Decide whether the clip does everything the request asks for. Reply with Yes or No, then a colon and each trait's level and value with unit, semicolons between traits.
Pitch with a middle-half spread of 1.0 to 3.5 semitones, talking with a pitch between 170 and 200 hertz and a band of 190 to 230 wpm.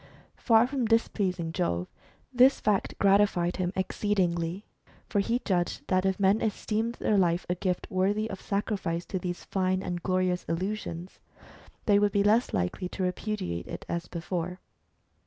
No: average, 2.8 semitones; high, 190 Hz; average, 155 wpm